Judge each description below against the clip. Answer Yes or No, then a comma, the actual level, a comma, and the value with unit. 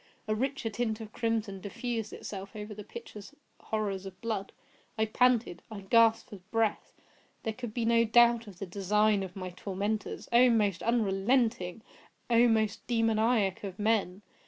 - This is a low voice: No, high, 215 Hz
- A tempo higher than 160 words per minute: No, average, 155 wpm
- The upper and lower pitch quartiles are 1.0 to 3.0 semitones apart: Yes, narrow, 2.6 semitones